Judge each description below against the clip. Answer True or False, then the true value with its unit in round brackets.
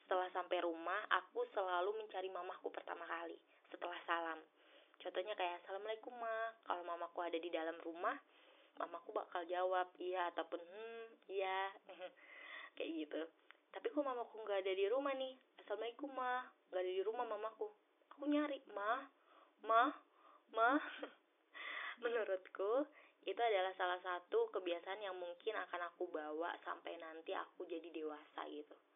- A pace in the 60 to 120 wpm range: False (140 wpm)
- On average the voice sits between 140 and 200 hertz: True (190 Hz)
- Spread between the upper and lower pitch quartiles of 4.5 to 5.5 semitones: True (5.0 semitones)